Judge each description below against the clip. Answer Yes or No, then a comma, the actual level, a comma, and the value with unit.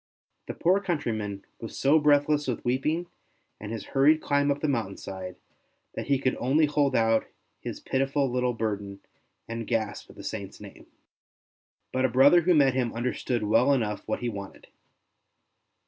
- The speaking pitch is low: Yes, low, 130 Hz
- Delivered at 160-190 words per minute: Yes, average, 165 wpm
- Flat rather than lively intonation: No, average, 4.3 semitones